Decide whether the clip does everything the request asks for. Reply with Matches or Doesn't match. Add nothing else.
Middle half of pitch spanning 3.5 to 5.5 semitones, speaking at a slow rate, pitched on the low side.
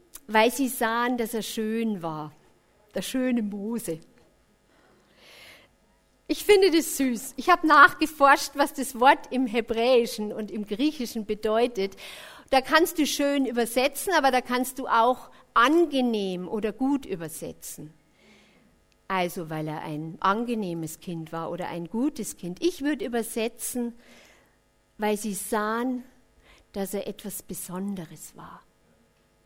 Doesn't match